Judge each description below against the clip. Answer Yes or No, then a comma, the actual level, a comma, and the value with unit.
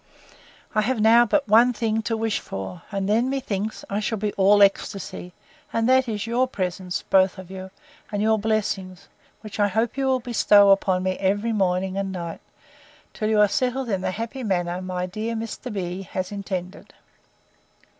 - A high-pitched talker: Yes, high, 205 Hz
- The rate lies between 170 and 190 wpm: Yes, average, 180 wpm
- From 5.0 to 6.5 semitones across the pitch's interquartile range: No, average, 3.2 semitones